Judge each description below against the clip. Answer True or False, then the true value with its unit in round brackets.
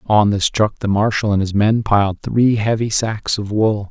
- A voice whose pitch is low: True (105 Hz)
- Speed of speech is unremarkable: False (215 wpm)